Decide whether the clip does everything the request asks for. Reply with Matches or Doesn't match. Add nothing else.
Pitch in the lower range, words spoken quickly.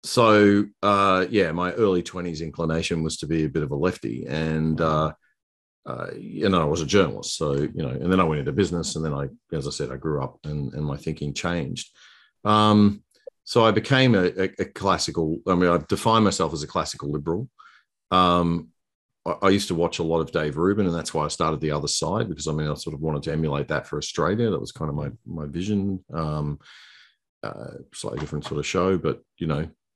Matches